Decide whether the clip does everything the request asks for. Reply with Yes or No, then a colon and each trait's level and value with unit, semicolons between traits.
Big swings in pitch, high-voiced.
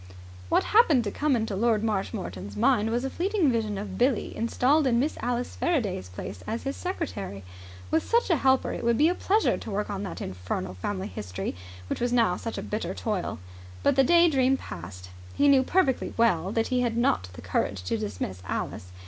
Yes: wide, 7.1 semitones; high, 230 Hz